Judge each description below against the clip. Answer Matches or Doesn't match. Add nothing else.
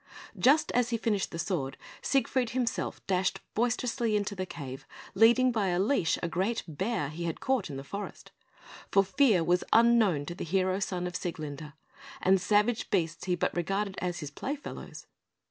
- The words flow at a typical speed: Matches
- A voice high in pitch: Matches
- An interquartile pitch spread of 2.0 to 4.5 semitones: Doesn't match